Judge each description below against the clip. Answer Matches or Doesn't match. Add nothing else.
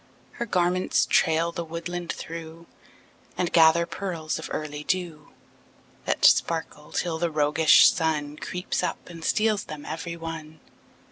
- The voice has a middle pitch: Matches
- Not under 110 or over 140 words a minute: Matches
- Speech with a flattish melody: Matches